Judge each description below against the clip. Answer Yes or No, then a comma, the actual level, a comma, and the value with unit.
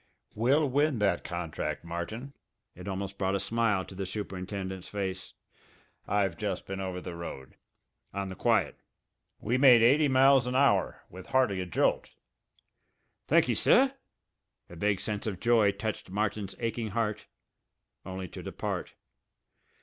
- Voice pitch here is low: Yes, low, 100 Hz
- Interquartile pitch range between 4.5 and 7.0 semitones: No, average, 3.8 semitones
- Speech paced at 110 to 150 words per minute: Yes, average, 140 wpm